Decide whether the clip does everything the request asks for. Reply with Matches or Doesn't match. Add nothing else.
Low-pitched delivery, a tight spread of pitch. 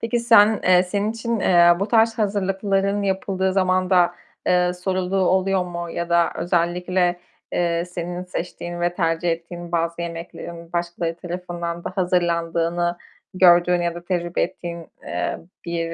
Doesn't match